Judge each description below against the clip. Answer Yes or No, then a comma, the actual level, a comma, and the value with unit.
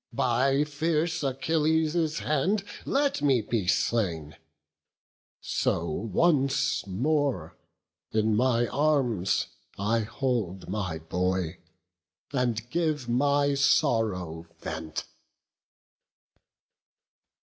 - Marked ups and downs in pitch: Yes, wide, 7.3 semitones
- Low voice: Yes, low, 125 Hz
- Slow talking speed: Yes, slow, 80 wpm